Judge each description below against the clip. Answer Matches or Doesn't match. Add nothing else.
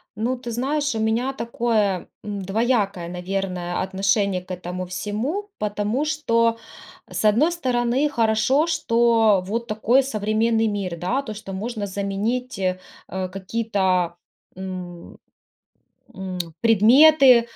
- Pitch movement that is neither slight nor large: Matches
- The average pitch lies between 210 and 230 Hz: Matches